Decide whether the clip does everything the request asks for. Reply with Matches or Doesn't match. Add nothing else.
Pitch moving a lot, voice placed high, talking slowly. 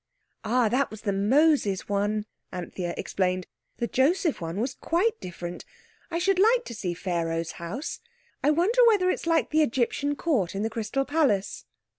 Doesn't match